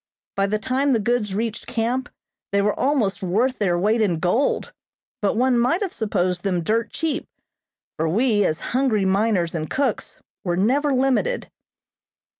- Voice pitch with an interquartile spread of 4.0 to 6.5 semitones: Yes, average, 5.0 semitones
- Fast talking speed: No, average, 160 wpm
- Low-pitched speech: No, high, 220 Hz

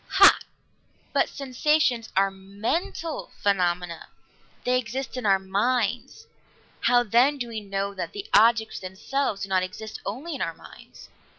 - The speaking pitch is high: Yes, high, 220 Hz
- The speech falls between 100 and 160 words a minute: Yes, average, 140 wpm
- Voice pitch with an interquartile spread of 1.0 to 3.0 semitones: No, average, 4.7 semitones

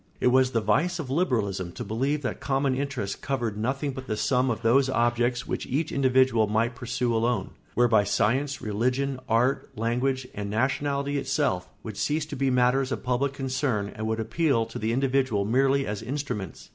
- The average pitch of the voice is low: Yes, low, 125 Hz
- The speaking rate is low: No, average, 180 wpm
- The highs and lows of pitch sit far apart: No, average, 3.5 semitones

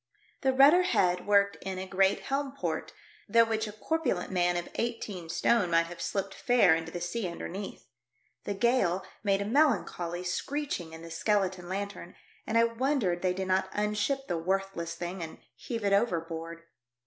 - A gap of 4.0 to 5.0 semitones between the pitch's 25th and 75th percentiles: Yes, average, 4.7 semitones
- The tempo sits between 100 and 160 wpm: No, average, 170 wpm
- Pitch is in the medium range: No, high, 195 Hz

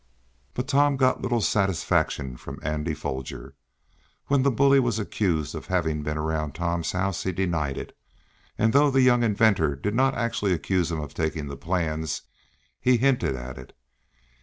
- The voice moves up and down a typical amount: No, wide, 7.8 semitones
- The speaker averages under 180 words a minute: Yes, average, 165 wpm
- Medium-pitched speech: No, very low, 90 Hz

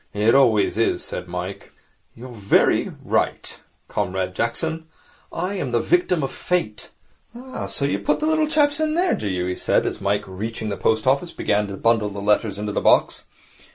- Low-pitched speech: Yes, low, 115 Hz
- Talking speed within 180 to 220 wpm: Yes, average, 190 wpm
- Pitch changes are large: Yes, wide, 8.7 semitones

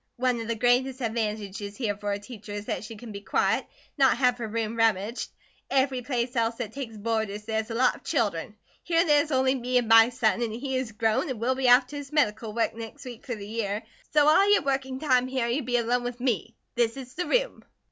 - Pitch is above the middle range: Yes, high, 240 Hz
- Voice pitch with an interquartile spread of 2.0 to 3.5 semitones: Yes, average, 2.9 semitones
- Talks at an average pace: No, fast, 240 wpm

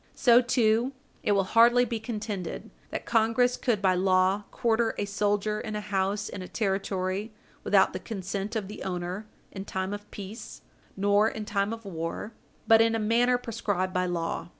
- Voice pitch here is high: Yes, high, 205 Hz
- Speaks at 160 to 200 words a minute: Yes, average, 175 wpm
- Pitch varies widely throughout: No, average, 2.8 semitones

